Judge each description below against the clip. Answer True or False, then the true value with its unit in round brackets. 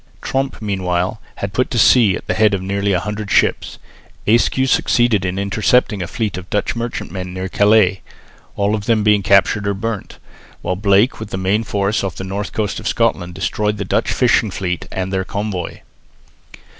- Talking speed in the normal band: True (185 wpm)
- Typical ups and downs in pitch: False (2.3 semitones)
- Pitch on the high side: False (100 Hz)